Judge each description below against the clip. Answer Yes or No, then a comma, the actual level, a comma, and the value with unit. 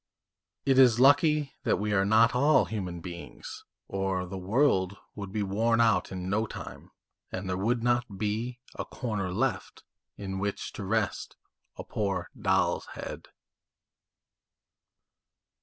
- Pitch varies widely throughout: No, average, 3.8 semitones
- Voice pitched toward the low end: Yes, low, 105 Hz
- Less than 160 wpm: Yes, average, 140 wpm